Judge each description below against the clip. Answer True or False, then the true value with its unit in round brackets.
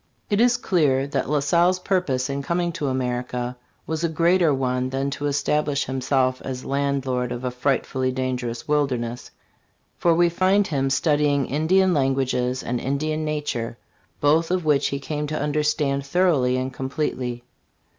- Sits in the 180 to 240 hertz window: False (140 Hz)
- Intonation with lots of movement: False (3.2 semitones)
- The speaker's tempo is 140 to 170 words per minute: True (165 wpm)